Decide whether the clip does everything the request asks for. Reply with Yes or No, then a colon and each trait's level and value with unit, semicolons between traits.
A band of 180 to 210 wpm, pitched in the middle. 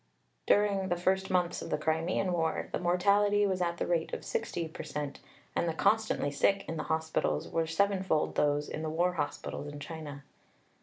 Yes: average, 190 wpm; medium, 170 Hz